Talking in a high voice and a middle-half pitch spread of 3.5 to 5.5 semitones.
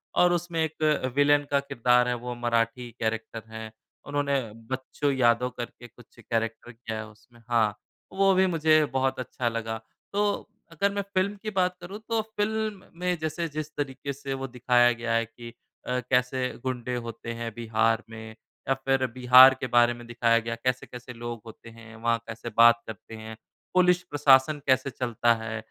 No: low, 125 Hz; average, 3.8 semitones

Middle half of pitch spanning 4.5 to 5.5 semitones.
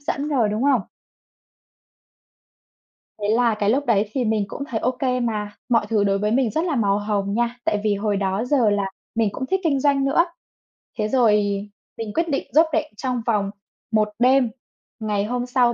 No: average, 3.9 semitones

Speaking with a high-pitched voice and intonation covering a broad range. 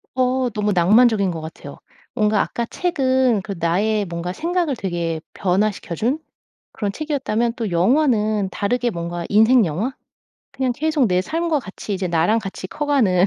Yes: high, 215 Hz; wide, 5.9 semitones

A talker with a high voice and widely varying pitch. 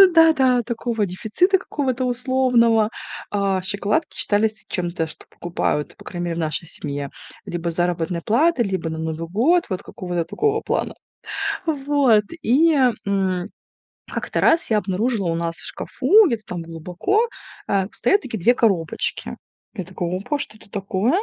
Yes: high, 205 Hz; wide, 6.7 semitones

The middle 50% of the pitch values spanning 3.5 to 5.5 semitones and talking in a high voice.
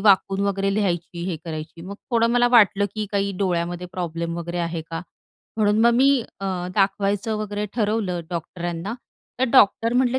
Yes: average, 3.8 semitones; high, 195 Hz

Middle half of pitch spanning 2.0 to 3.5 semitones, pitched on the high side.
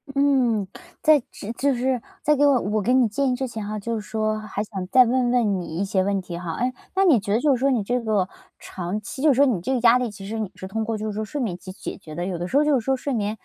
No: average, 4.3 semitones; high, 220 Hz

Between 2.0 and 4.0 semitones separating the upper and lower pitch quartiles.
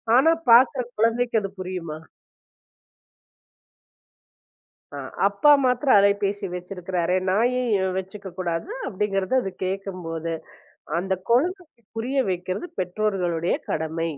No: average, 4.4 semitones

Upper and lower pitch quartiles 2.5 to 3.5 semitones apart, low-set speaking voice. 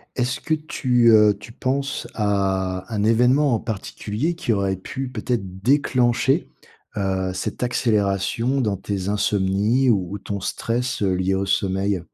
No: average, 4.2 semitones; low, 105 Hz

